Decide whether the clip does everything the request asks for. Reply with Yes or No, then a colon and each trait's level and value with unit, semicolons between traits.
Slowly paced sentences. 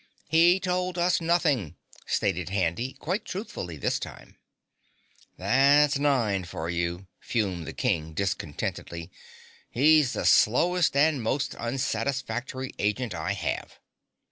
Yes: slow, 115 wpm